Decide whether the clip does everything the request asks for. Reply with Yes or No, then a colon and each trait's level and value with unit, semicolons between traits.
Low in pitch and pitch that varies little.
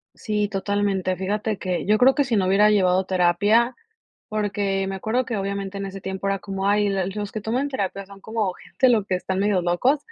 No: high, 200 Hz; narrow, 1.9 semitones